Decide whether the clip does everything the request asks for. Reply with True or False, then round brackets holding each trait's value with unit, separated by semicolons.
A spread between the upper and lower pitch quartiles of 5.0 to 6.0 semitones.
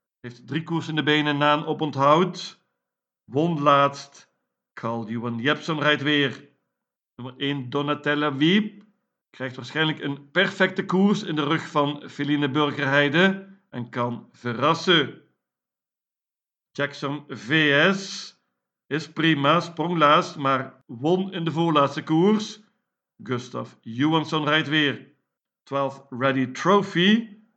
False (3.6 semitones)